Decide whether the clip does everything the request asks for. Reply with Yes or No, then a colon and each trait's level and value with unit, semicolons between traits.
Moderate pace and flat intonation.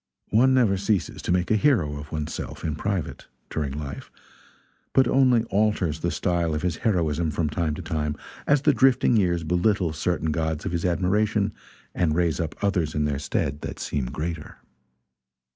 No: average, 175 wpm; average, 5.0 semitones